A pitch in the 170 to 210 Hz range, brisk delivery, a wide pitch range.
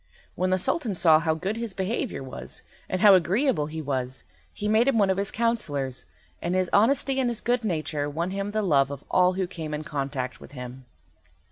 Yes: medium, 185 Hz; fast, 210 wpm; wide, 6.5 semitones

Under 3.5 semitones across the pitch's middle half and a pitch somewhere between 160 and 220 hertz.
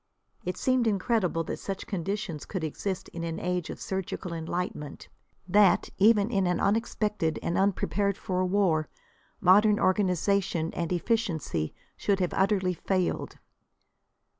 Yes: average, 2.8 semitones; medium, 185 Hz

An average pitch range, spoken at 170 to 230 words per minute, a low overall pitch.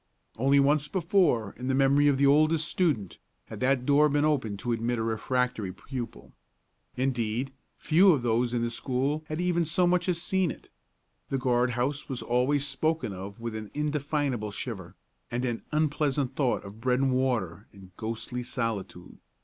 Yes: average, 4.2 semitones; average, 175 wpm; low, 130 Hz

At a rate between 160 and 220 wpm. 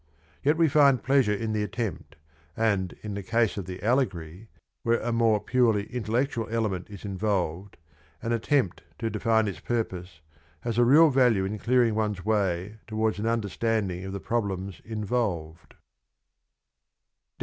No: average, 150 wpm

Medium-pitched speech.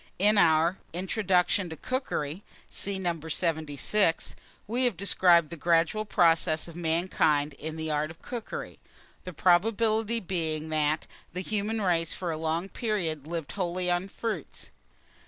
Yes: medium, 175 Hz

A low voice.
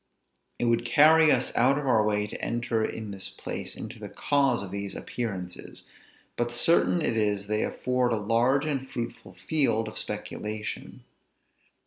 Yes: low, 115 Hz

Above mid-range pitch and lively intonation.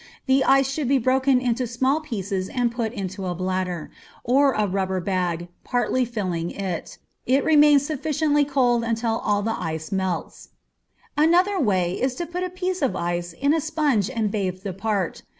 Yes: high, 235 Hz; wide, 6.7 semitones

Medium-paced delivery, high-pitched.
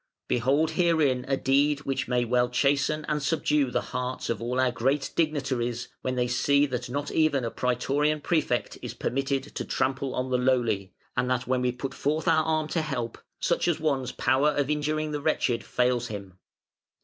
No: average, 185 wpm; low, 135 Hz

